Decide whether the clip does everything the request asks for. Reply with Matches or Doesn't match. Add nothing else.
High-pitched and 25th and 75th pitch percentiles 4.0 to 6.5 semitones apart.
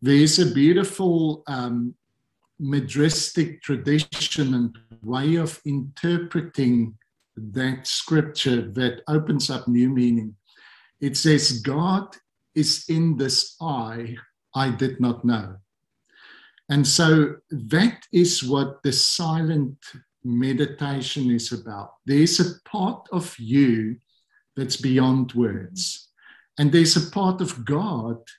Doesn't match